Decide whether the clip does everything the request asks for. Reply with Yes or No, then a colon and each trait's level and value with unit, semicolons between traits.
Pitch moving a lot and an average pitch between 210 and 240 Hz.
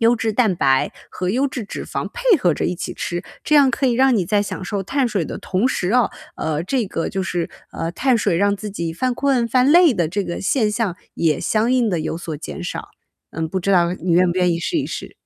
No: wide, 6.3 semitones; high, 200 Hz